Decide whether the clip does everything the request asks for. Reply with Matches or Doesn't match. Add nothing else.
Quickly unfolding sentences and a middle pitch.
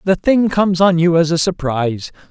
Matches